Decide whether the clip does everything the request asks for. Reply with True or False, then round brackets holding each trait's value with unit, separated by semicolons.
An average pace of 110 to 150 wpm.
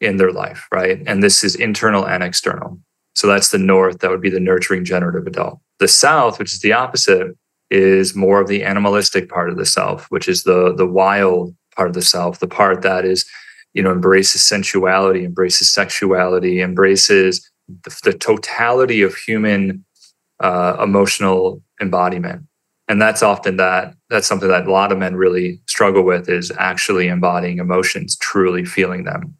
False (175 wpm)